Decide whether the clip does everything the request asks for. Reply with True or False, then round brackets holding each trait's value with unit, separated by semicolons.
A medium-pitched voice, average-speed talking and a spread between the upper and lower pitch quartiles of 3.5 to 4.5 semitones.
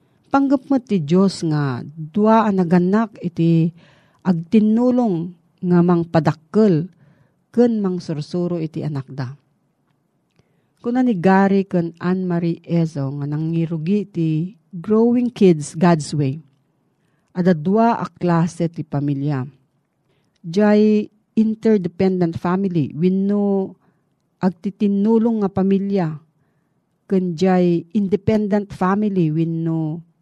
False (175 Hz; 100 wpm; 4.0 semitones)